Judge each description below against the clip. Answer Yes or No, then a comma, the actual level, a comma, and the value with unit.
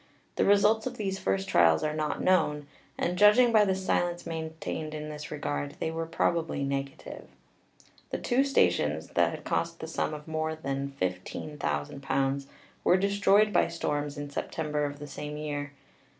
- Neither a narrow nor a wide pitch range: Yes, average, 3.9 semitones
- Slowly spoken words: No, average, 165 wpm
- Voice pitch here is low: No, medium, 155 Hz